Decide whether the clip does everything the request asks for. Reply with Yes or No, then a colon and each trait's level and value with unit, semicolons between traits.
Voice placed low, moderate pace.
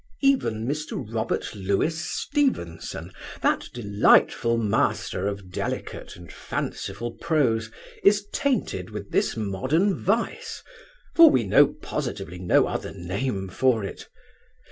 No: low, 115 Hz; slow, 115 wpm